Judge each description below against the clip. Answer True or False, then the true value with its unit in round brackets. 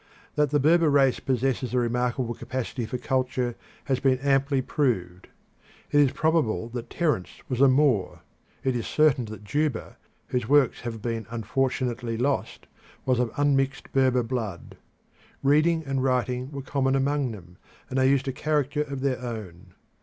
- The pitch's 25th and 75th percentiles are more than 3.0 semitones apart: False (2.7 semitones)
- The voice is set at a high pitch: False (130 Hz)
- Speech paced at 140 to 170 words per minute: True (160 wpm)